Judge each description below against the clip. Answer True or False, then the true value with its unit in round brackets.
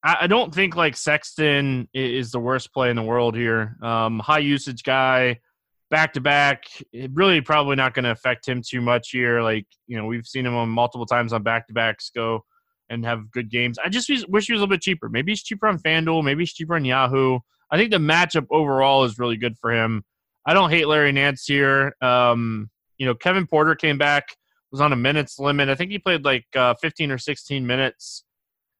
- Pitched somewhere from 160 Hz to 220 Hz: False (135 Hz)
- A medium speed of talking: False (215 wpm)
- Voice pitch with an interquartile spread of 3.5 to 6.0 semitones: True (4.3 semitones)